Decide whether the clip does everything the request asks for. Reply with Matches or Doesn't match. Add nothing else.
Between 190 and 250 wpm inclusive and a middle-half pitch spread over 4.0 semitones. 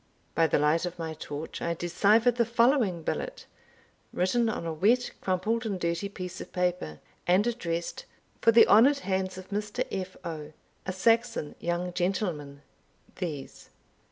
Doesn't match